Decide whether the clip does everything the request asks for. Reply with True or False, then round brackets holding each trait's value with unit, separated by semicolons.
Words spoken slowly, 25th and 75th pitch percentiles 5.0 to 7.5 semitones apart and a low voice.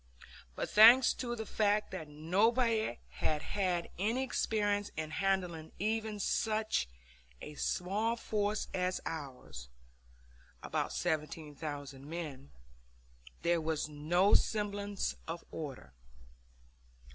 False (100 wpm; 5.6 semitones; 185 Hz)